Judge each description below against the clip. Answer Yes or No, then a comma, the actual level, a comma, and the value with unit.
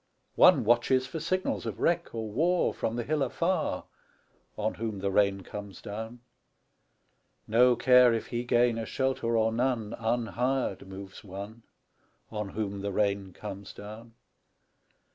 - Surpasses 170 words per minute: No, average, 145 wpm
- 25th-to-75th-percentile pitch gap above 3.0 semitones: Yes, average, 3.4 semitones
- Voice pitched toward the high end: No, low, 115 Hz